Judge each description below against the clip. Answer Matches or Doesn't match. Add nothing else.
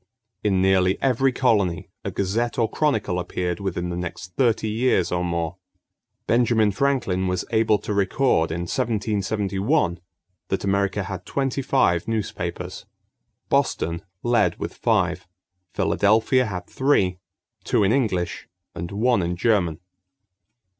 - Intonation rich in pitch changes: Doesn't match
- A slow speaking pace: Matches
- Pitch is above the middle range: Doesn't match